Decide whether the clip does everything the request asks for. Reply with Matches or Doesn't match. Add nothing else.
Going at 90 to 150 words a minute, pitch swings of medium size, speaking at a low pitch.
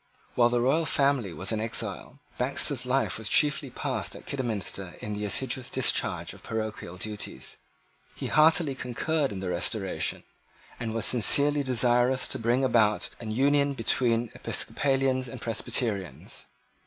Matches